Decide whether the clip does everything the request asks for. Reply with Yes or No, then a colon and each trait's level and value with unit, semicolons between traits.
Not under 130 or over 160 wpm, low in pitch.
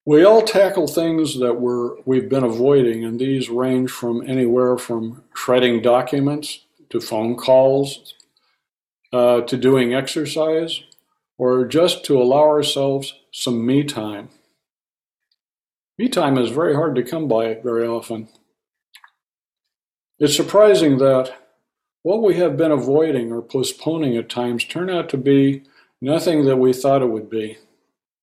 Yes: average, 140 wpm; low, 130 Hz